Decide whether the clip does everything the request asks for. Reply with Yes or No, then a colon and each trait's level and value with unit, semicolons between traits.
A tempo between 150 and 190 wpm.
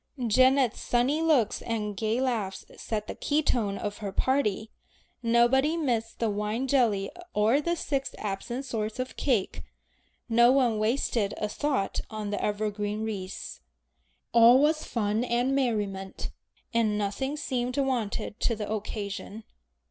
No: average, 140 wpm